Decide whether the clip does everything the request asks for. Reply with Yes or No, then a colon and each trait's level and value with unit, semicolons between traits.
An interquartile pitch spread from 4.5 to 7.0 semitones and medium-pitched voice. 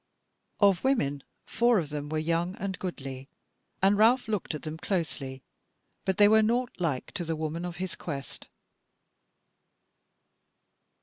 Yes: average, 5.0 semitones; medium, 175 Hz